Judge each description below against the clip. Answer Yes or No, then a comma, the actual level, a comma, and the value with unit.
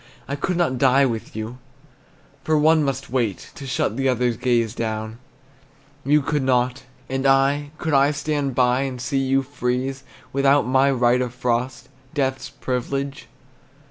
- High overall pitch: No, low, 130 Hz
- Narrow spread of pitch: Yes, narrow, 2.0 semitones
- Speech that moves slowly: No, average, 155 wpm